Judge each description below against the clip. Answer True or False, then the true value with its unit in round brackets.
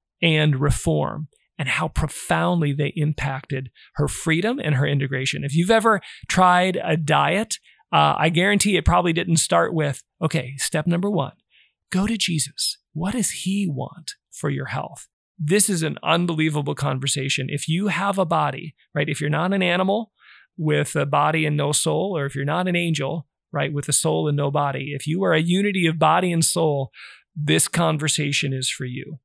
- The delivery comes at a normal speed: True (185 wpm)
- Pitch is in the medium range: True (155 Hz)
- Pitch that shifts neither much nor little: True (3.6 semitones)